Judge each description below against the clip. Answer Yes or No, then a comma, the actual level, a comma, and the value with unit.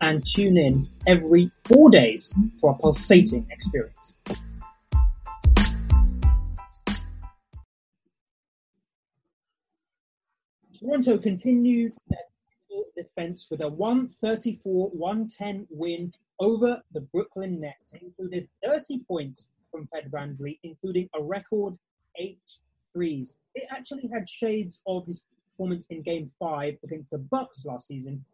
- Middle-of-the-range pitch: Yes, medium, 175 Hz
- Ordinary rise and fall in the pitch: No, wide, 6.1 semitones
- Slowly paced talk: Yes, slow, 105 wpm